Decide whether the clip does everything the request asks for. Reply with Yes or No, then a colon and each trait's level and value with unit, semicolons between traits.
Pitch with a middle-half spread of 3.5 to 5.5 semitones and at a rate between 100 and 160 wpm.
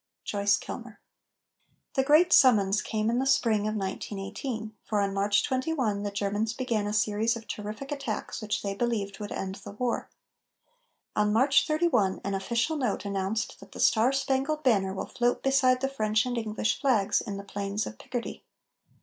No: average, 4.0 semitones; average, 175 wpm